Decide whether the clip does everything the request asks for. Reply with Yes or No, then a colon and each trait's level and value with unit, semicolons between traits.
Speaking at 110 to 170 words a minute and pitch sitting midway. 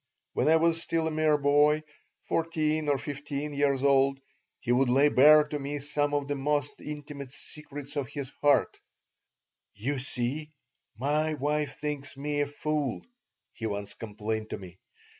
Yes: average, 160 wpm; medium, 145 Hz